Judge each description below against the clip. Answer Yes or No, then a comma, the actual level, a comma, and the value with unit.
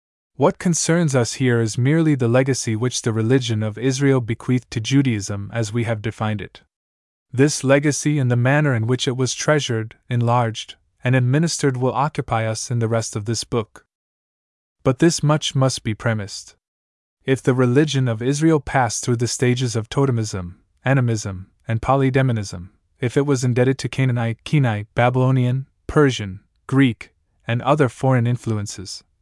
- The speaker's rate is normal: Yes, average, 160 wpm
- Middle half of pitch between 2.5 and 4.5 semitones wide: Yes, average, 3.3 semitones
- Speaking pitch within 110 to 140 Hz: Yes, low, 125 Hz